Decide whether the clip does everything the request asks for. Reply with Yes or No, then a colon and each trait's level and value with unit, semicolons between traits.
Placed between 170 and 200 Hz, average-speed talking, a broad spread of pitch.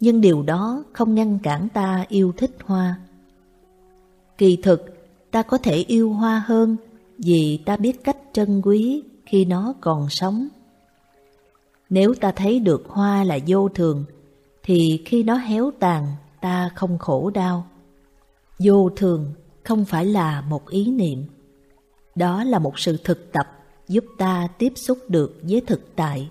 No: medium, 185 Hz; slow, 155 wpm; wide, 5.7 semitones